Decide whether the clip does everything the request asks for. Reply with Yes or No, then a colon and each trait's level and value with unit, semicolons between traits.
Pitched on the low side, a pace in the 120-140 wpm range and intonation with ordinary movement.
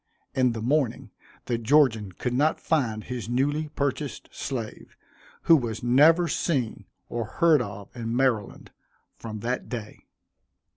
Yes: low, 125 Hz; slow, 135 wpm; average, 4.3 semitones